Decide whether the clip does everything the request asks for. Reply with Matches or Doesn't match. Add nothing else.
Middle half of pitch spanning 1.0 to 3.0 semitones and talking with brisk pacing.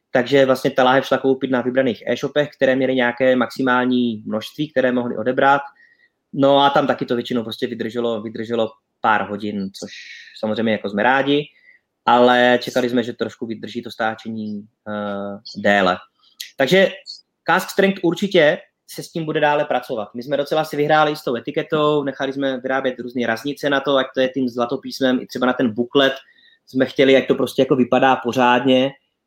Matches